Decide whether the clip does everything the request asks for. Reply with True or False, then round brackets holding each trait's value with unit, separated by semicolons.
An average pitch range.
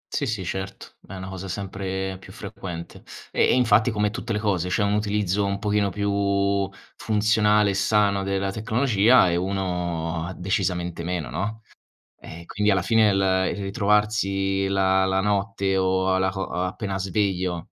False (1.8 semitones)